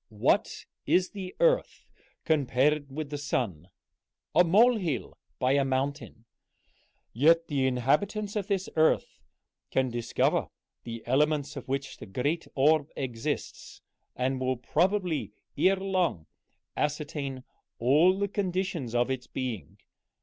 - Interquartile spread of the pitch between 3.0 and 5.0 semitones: No, wide, 5.6 semitones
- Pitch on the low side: No, medium, 145 Hz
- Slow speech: Yes, slow, 120 wpm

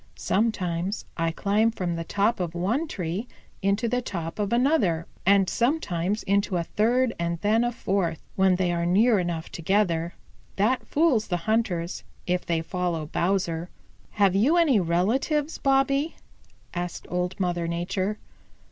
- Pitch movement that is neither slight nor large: Yes, average, 4.7 semitones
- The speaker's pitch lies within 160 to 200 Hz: Yes, high, 190 Hz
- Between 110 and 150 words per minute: Yes, average, 145 wpm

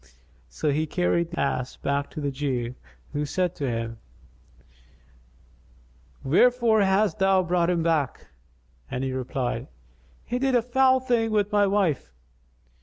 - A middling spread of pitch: No, wide, 7.0 semitones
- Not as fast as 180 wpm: Yes, average, 140 wpm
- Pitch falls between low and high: Yes, medium, 170 Hz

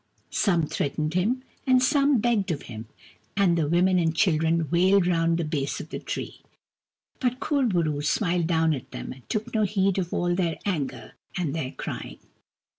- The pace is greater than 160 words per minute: Yes, average, 185 wpm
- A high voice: No, medium, 175 Hz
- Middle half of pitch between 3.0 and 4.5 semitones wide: Yes, average, 3.8 semitones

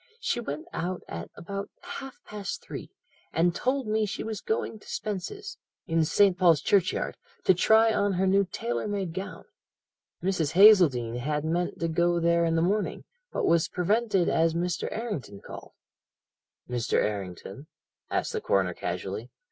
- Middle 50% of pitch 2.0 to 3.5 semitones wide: No, average, 4.4 semitones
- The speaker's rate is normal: Yes, average, 155 wpm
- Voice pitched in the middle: Yes, medium, 180 Hz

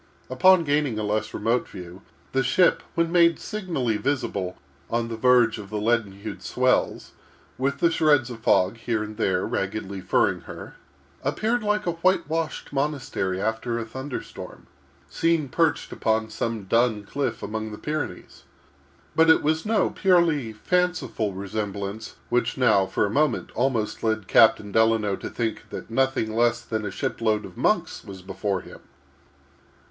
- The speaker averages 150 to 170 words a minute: Yes, average, 160 wpm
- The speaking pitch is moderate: No, low, 115 Hz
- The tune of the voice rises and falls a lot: Yes, wide, 5.8 semitones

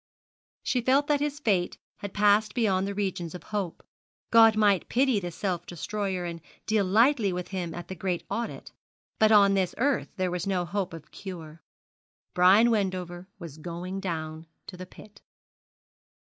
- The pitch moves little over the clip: No, average, 3.2 semitones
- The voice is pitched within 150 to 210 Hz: Yes, high, 190 Hz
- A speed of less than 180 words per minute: Yes, average, 165 wpm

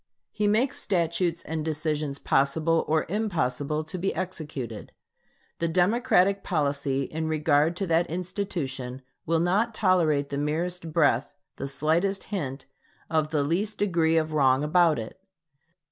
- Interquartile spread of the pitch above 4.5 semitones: No, average, 3.7 semitones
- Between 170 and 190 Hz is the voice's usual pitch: No, medium, 160 Hz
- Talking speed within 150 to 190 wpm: No, slow, 135 wpm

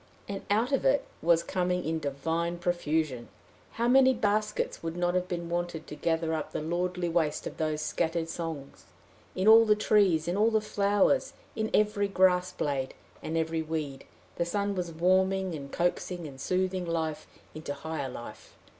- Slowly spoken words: No, average, 170 wpm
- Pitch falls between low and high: Yes, medium, 175 Hz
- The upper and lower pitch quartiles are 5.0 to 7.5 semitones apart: No, average, 3.5 semitones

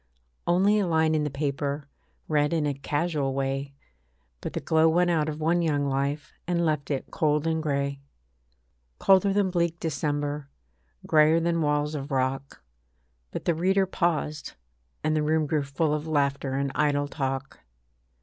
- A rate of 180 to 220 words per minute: No, average, 160 wpm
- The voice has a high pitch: No, medium, 150 Hz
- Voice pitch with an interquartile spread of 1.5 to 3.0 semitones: Yes, narrow, 2.6 semitones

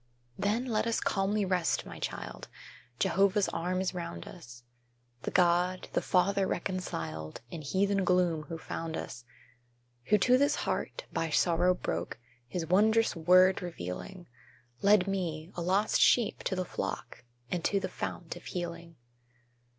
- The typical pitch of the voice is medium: Yes, medium, 180 Hz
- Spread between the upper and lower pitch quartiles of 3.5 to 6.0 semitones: No, average, 2.9 semitones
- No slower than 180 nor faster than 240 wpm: No, average, 145 wpm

